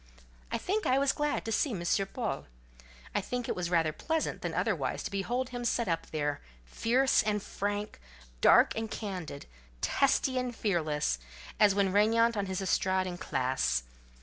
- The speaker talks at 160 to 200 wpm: Yes, average, 170 wpm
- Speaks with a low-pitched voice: No, high, 205 Hz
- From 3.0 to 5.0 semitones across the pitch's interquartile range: No, wide, 5.6 semitones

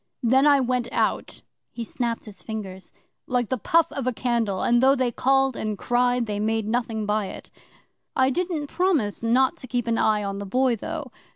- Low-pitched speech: No, high, 240 Hz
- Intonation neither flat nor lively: Yes, average, 3.3 semitones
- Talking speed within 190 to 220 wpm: Yes, average, 195 wpm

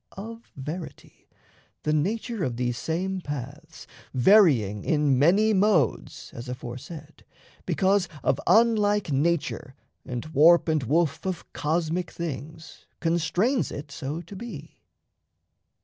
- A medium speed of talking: No, slow, 115 wpm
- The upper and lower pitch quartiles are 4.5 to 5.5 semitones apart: Yes, average, 5.2 semitones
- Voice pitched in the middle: Yes, medium, 160 Hz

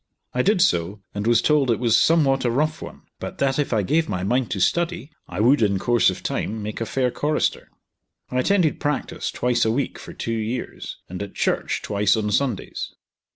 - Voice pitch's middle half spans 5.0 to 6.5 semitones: Yes, wide, 5.6 semitones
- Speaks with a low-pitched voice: Yes, low, 120 Hz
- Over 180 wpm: Yes, fast, 205 wpm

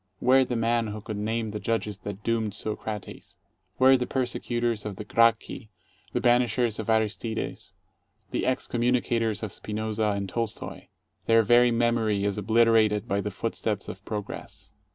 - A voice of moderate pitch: No, low, 110 Hz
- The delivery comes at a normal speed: Yes, average, 155 wpm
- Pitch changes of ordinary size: No, narrow, 2.0 semitones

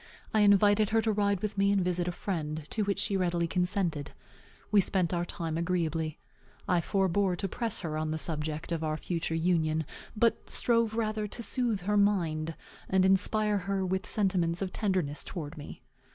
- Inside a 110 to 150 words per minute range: No, average, 180 wpm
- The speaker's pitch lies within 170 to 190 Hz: Yes, medium, 185 Hz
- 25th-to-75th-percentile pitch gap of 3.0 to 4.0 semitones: Yes, average, 3.7 semitones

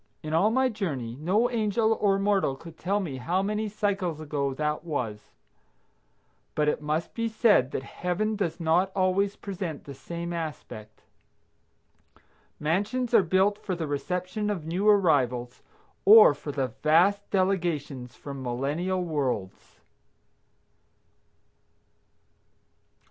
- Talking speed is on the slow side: Yes, slow, 125 wpm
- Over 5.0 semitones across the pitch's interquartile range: Yes, wide, 5.6 semitones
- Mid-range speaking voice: Yes, medium, 175 Hz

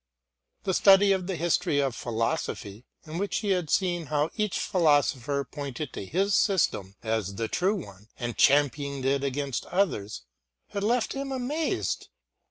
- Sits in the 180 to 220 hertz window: No, medium, 150 Hz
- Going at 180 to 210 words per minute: No, average, 155 wpm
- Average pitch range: No, wide, 7.2 semitones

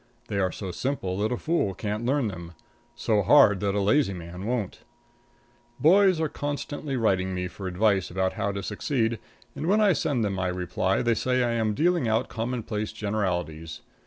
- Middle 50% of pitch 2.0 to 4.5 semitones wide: No, average, 5.2 semitones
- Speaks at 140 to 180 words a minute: No, average, 190 wpm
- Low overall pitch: Yes, low, 105 Hz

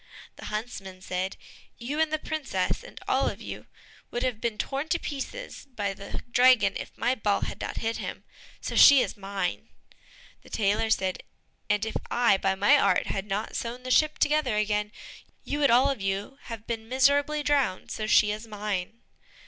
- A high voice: Yes, high, 225 Hz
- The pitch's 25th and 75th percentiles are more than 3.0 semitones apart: Yes, average, 5.0 semitones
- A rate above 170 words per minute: Yes, average, 185 wpm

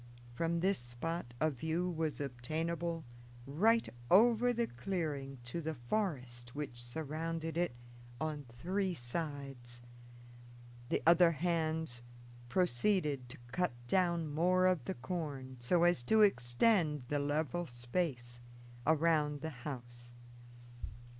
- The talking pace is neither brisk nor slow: No, slow, 115 wpm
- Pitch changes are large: Yes, wide, 5.7 semitones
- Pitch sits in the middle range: Yes, medium, 155 Hz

